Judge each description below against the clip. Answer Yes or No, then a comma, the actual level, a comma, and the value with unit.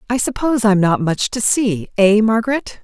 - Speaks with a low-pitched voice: No, high, 215 Hz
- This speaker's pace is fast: Yes, fast, 210 wpm